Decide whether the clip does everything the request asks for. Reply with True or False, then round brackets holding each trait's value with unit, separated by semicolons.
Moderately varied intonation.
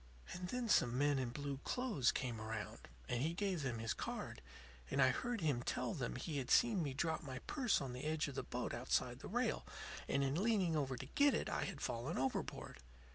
False (5.8 semitones)